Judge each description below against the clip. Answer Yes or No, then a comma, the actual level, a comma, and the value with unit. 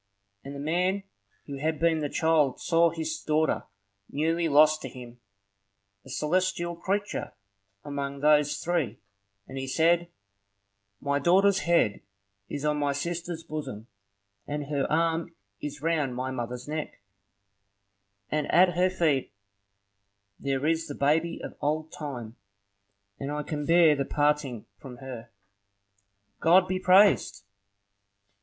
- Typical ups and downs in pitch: Yes, average, 3.1 semitones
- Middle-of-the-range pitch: Yes, medium, 150 Hz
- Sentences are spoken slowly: Yes, slow, 130 wpm